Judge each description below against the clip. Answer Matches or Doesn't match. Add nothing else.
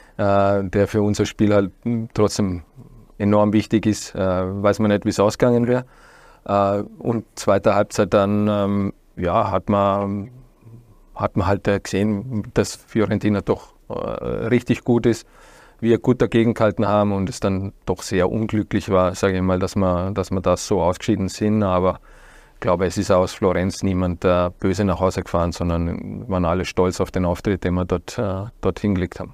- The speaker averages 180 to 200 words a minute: Doesn't match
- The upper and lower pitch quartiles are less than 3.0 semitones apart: Matches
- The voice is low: Matches